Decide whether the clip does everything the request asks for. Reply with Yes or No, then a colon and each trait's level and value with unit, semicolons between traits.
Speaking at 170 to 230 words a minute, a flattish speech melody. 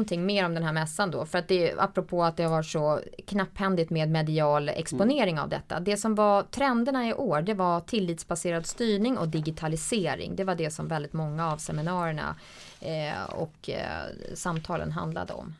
No: average, 175 wpm; average, 3.9 semitones